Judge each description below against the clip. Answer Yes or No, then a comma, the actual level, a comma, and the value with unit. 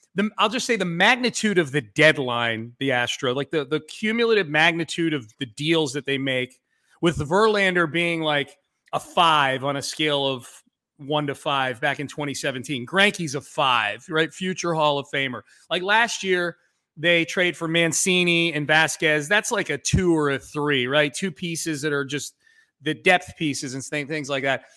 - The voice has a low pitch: No, medium, 155 Hz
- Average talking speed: Yes, average, 180 wpm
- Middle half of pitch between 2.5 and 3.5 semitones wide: No, average, 3.9 semitones